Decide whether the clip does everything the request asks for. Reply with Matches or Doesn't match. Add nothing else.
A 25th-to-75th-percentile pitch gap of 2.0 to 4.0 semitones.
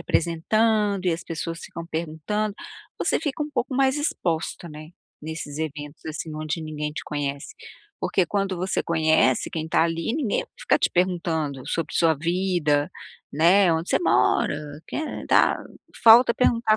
Doesn't match